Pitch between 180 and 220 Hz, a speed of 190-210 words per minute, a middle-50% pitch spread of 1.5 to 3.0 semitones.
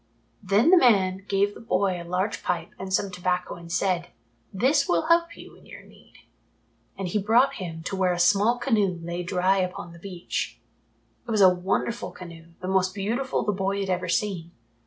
Yes: high, 190 Hz; average, 200 wpm; narrow, 2.5 semitones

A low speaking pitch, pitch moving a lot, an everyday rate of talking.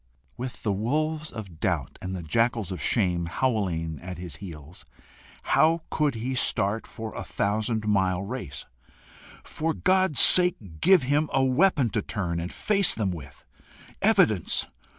Yes: low, 110 Hz; wide, 7.6 semitones; average, 150 wpm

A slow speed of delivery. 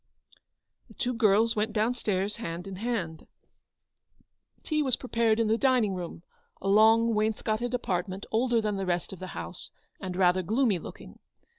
No: average, 160 wpm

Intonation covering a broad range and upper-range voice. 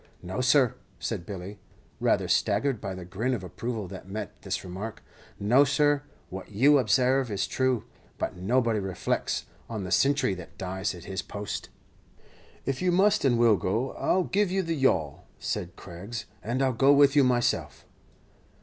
No: wide, 6.1 semitones; low, 115 Hz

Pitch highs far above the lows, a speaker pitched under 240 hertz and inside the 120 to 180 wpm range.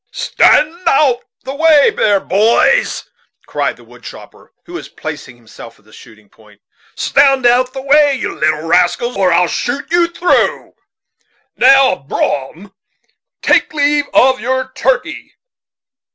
No: wide, 8.8 semitones; very high, 255 Hz; average, 150 wpm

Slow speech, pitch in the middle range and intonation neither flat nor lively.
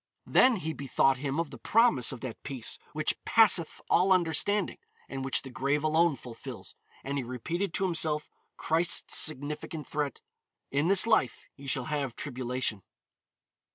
No: average, 155 wpm; medium, 150 Hz; average, 4.1 semitones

